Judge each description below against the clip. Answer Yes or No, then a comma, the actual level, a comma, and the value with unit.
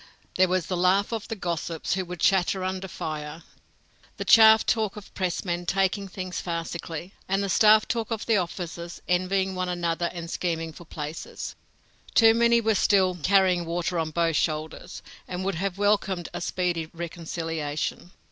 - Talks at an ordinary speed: Yes, average, 175 wpm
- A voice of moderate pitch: Yes, medium, 180 Hz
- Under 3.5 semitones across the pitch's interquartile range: Yes, narrow, 2.6 semitones